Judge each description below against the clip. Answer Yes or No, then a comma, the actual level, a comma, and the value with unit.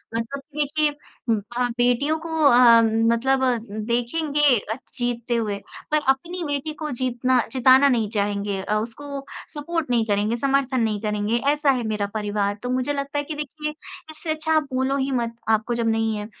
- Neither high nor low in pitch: No, very high, 250 Hz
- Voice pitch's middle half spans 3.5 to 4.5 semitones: Yes, average, 4.2 semitones